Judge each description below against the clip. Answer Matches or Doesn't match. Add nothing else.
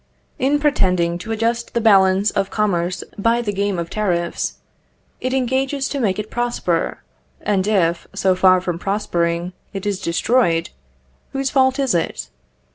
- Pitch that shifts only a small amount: Doesn't match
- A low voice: Doesn't match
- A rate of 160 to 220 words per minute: Doesn't match